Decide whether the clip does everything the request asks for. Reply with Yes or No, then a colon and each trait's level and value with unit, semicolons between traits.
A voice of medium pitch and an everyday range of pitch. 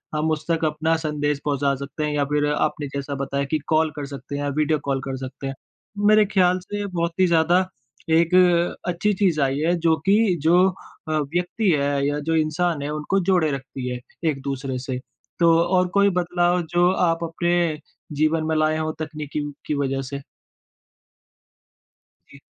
Yes: medium, 155 Hz; average, 3.5 semitones